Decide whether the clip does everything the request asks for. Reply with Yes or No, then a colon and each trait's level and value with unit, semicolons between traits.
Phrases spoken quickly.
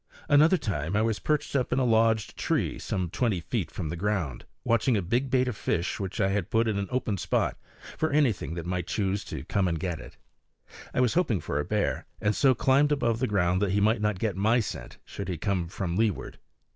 Yes: fast, 230 wpm